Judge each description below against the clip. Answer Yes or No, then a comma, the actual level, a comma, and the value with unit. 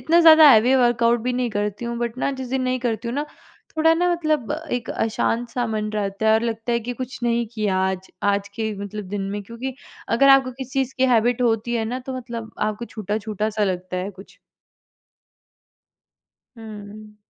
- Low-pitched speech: No, high, 230 Hz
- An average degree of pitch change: Yes, average, 3.0 semitones